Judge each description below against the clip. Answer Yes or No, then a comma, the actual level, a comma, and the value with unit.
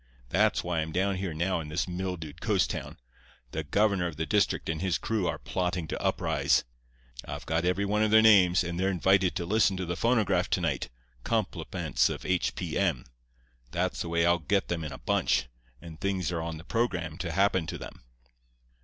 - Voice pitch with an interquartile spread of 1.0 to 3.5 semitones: Yes, average, 2.9 semitones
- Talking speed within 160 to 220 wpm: Yes, fast, 205 wpm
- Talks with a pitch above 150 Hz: No, very low, 90 Hz